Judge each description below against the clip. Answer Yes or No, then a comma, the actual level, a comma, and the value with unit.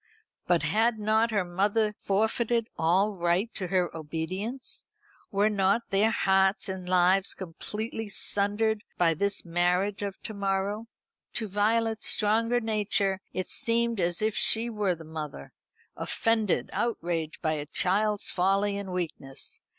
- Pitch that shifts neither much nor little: Yes, average, 3.4 semitones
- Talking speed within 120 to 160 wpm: Yes, slow, 135 wpm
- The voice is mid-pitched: No, high, 200 Hz